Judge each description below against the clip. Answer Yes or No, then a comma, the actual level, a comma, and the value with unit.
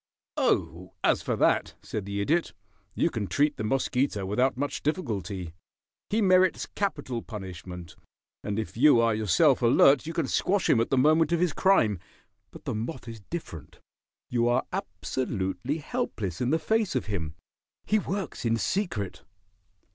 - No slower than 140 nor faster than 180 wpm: Yes, average, 160 wpm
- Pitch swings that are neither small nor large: No, wide, 7.9 semitones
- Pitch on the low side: Yes, low, 125 Hz